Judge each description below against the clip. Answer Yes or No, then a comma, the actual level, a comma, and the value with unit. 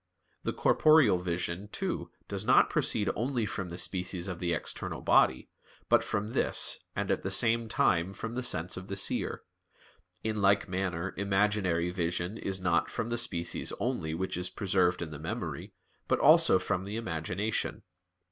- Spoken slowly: No, average, 165 wpm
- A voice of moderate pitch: No, very low, 95 Hz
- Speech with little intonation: No, average, 3.3 semitones